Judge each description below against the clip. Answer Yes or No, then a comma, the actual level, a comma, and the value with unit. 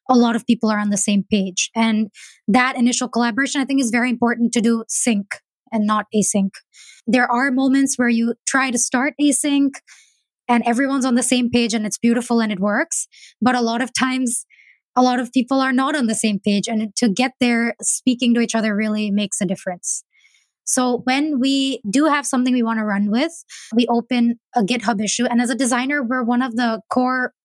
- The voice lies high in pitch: Yes, high, 240 Hz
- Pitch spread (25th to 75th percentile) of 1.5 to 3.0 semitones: Yes, narrow, 2.5 semitones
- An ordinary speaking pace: No, fast, 210 wpm